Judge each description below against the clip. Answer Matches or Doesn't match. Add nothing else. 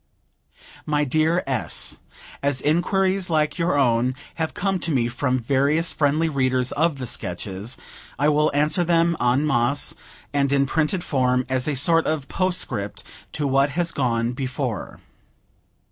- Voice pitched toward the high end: Doesn't match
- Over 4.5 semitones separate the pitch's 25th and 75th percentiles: Doesn't match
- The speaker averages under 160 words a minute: Matches